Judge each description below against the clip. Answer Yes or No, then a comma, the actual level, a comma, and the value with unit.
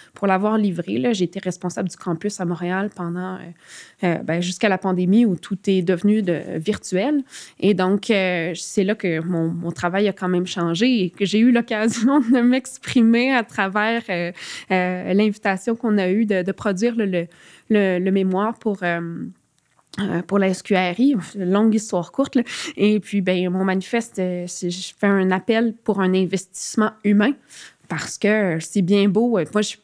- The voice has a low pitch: No, high, 195 Hz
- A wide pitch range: No, average, 2.9 semitones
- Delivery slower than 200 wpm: Yes, average, 180 wpm